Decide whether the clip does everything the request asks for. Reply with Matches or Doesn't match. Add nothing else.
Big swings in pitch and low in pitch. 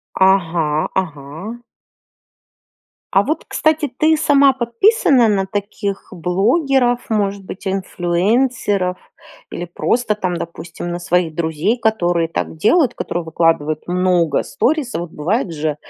Doesn't match